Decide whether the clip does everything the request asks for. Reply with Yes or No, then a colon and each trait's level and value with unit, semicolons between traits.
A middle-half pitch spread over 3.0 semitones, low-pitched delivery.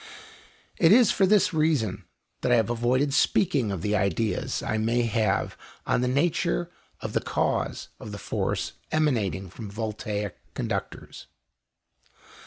Yes: wide, 5.5 semitones; low, 115 Hz